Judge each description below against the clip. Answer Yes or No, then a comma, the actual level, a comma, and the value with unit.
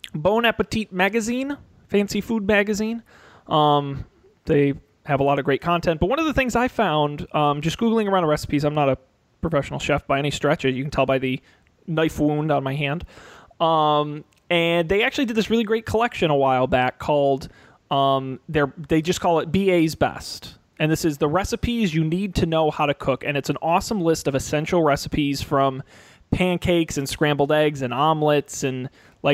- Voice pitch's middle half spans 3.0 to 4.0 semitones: No, average, 4.4 semitones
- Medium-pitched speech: Yes, medium, 150 Hz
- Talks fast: No, average, 190 wpm